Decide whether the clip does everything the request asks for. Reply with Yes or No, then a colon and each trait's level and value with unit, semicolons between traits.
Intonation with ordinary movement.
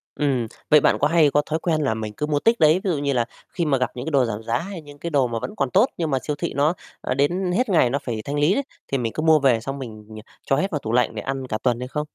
Yes: average, 4.0 semitones